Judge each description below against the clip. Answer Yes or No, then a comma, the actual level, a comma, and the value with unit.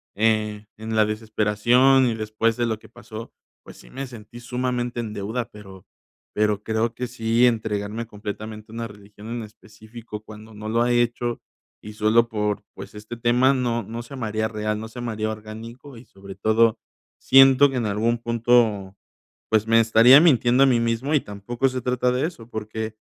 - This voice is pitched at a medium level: No, low, 115 Hz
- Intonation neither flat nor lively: No, narrow, 2.0 semitones